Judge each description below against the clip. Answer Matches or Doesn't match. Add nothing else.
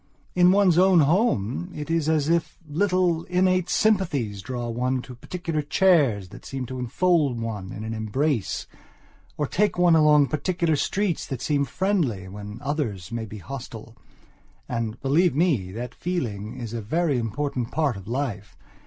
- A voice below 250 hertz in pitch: Matches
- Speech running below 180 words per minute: Matches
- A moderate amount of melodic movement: Doesn't match